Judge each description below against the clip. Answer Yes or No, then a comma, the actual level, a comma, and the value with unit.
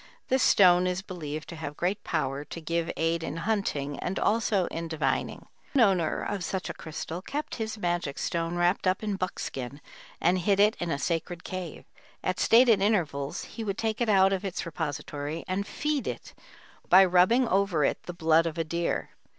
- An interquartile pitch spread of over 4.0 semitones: No, average, 3.4 semitones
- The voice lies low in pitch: No, medium, 180 Hz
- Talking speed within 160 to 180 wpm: No, average, 190 wpm